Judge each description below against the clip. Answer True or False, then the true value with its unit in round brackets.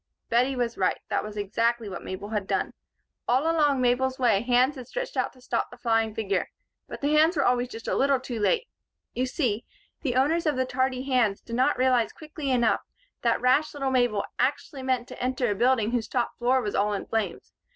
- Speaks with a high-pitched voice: True (250 Hz)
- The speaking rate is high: True (215 wpm)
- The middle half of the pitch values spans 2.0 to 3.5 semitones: True (2.5 semitones)